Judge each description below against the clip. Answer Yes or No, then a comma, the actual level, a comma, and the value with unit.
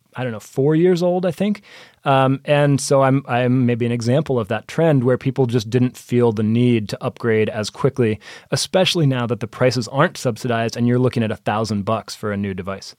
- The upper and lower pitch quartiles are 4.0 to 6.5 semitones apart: No, average, 3.2 semitones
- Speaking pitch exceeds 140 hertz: No, low, 125 Hz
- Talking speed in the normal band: No, fast, 220 wpm